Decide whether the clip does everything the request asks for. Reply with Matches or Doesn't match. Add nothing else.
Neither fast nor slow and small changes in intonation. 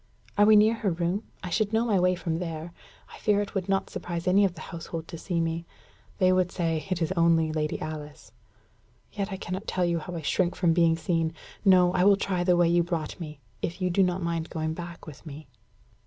Doesn't match